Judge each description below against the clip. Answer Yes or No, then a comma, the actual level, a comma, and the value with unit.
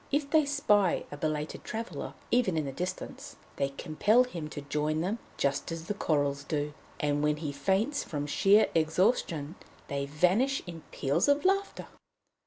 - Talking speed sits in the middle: Yes, average, 165 wpm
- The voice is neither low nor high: Yes, medium, 165 Hz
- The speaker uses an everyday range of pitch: No, wide, 6.7 semitones